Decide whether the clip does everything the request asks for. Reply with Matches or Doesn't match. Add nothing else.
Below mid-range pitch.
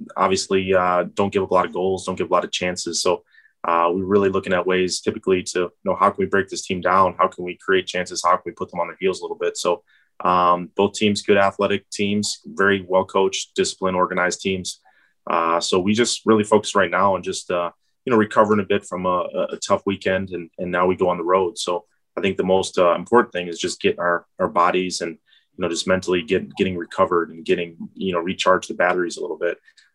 Matches